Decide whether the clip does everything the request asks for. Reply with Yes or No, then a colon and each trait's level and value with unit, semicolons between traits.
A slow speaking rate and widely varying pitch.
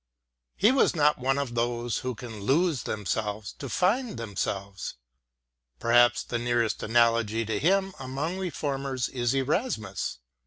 No: slow, 130 wpm; average, 4.6 semitones